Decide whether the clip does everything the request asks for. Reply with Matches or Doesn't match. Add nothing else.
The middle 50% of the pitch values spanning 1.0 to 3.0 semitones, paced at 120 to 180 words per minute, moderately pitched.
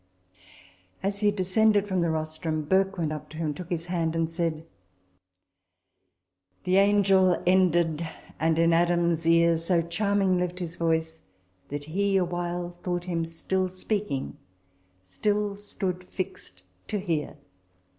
Matches